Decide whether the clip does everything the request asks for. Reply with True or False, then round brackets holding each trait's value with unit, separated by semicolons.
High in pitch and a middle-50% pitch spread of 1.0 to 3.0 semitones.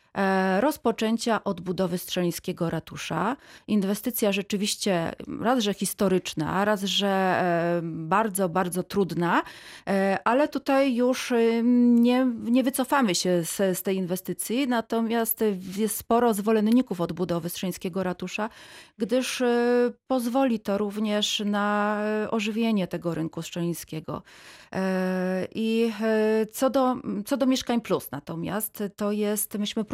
False (210 Hz; 4.0 semitones)